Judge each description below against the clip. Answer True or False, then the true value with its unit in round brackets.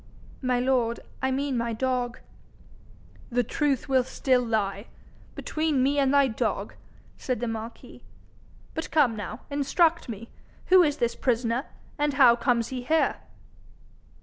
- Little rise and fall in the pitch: False (3.1 semitones)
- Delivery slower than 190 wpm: True (140 wpm)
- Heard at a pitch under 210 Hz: False (255 Hz)